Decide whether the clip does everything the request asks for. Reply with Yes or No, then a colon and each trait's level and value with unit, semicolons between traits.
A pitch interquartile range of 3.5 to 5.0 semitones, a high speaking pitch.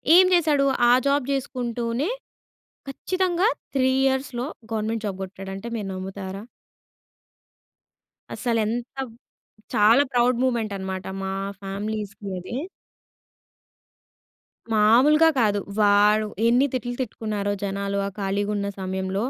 Yes: average, 4.2 semitones; high, 215 Hz